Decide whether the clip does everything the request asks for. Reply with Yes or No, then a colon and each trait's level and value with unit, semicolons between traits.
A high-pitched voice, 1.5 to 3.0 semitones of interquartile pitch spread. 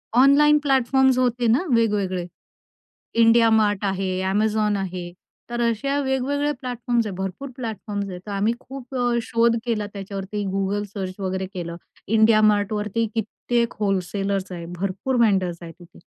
No: high, 215 Hz; average, 3.7 semitones